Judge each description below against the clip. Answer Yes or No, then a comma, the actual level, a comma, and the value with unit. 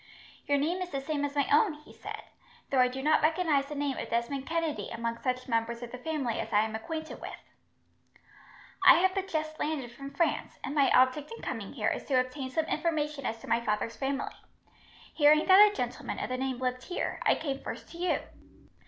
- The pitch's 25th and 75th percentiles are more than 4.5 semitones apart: No, average, 3.7 semitones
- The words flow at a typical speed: No, fast, 215 wpm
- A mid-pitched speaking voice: No, very high, 280 Hz